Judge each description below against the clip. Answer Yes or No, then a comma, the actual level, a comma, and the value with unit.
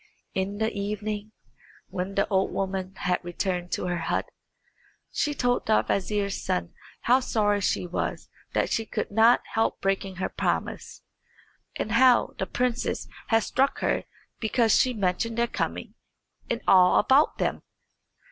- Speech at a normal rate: Yes, average, 145 wpm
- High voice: Yes, high, 205 Hz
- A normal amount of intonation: Yes, average, 3.4 semitones